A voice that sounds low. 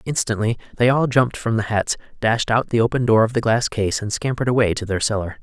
Yes: low, 115 Hz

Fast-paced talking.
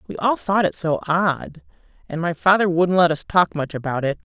Yes: fast, 225 wpm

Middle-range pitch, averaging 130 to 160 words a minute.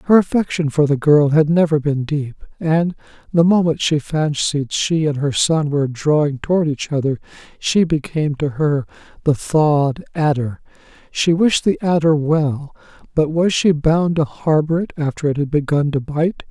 No: medium, 150 Hz; average, 175 wpm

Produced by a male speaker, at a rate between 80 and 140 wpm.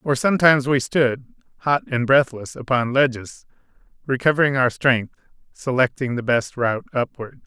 Yes: male; slow, 135 wpm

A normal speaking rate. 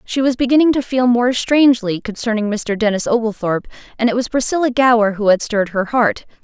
Yes: average, 195 wpm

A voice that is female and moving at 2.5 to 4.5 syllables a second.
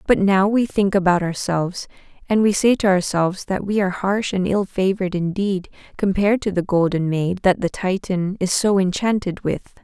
No: female; 5.2 syllables/s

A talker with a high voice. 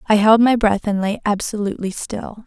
Yes: high, 210 Hz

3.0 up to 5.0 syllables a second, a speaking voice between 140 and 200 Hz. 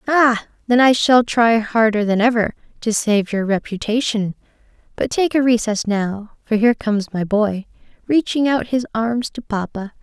No: 4.6 syllables/s; high, 225 Hz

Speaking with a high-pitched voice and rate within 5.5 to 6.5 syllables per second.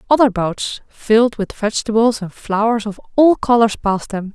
No: high, 220 Hz; 5.1 syllables/s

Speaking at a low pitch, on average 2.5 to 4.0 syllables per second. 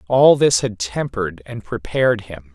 No: low, 110 Hz; 4.7 syllables/s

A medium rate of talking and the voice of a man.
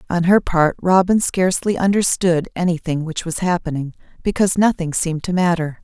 No: average, 155 wpm; female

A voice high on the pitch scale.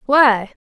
Yes: high, 245 Hz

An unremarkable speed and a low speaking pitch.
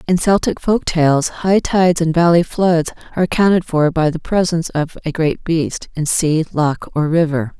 No: average, 190 wpm; medium, 165 Hz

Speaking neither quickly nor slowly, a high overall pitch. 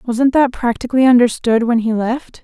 Yes: average, 175 wpm; high, 240 Hz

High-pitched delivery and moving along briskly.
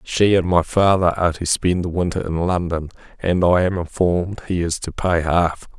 No: very low, 85 Hz; fast, 210 wpm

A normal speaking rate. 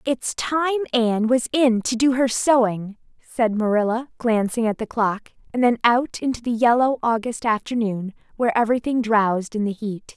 Yes: average, 170 wpm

